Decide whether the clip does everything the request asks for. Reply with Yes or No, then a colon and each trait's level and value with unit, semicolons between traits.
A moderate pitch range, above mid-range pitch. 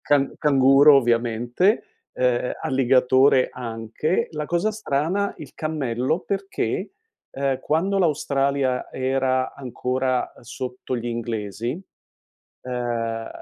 No: average, 3.6 semitones; low, 130 Hz